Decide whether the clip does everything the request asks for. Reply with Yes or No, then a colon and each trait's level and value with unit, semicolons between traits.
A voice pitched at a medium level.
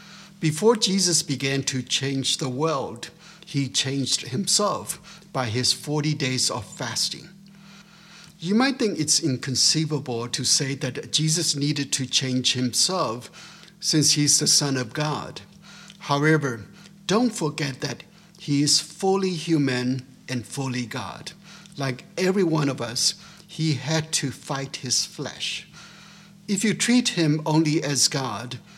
Yes: medium, 155 Hz